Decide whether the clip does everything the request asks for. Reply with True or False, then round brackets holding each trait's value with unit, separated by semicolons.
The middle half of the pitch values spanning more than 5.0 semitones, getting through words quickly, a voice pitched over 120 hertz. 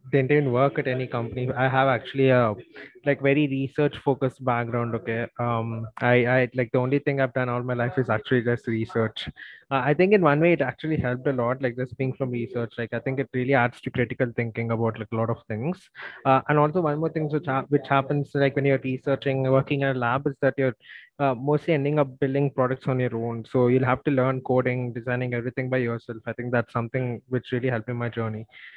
False (2.5 semitones; 235 wpm; 130 Hz)